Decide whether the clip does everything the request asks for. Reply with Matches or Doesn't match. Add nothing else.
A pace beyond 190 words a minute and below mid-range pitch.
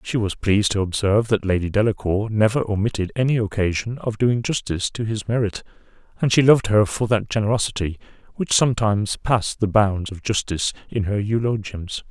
Doesn't match